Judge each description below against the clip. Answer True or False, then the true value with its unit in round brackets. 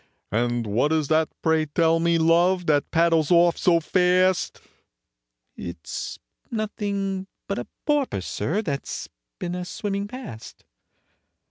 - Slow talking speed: True (130 wpm)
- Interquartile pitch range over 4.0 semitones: False (3.4 semitones)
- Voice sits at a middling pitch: True (170 Hz)